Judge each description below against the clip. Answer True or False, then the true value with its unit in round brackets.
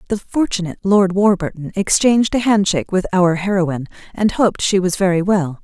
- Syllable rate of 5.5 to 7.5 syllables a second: True (5.8 syllables/s)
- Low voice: False (190 Hz)